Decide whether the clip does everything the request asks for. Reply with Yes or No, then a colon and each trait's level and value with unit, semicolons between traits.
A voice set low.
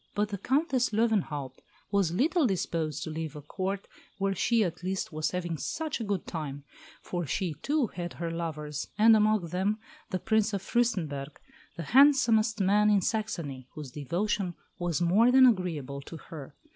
No: medium, 185 Hz